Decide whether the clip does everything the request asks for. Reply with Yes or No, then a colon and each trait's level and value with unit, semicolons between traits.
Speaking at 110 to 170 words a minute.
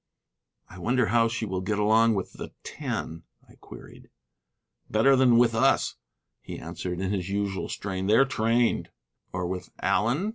Yes: average, 155 wpm